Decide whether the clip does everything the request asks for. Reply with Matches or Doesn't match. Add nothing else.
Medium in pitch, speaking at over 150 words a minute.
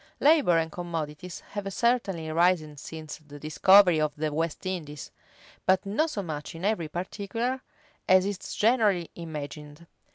Doesn't match